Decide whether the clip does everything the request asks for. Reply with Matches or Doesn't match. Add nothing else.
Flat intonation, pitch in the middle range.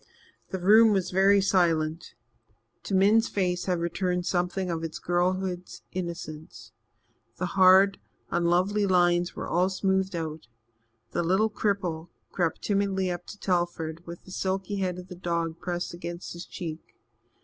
Matches